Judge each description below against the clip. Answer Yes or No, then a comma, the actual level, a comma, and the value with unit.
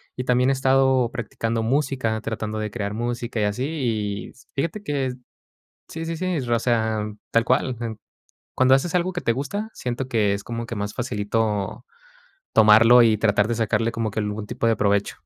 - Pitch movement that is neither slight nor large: Yes, average, 3.4 semitones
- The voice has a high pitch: No, low, 115 Hz